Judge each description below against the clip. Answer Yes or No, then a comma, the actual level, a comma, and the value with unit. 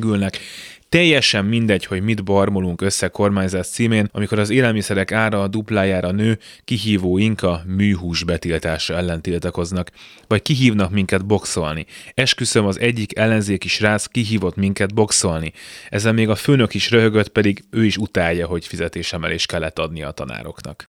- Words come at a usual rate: Yes, average, 145 wpm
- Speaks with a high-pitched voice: No, low, 100 Hz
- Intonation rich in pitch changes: No, average, 3.5 semitones